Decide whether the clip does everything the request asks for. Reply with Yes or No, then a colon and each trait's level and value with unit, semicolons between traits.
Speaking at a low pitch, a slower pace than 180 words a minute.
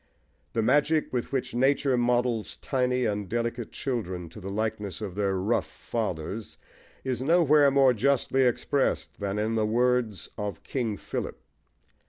Yes: low, 120 Hz; average, 145 wpm